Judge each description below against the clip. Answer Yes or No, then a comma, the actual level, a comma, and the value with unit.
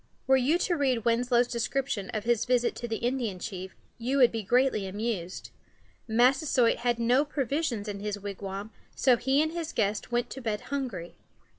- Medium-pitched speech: No, high, 240 Hz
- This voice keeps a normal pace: Yes, average, 175 wpm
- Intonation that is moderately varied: Yes, average, 4.0 semitones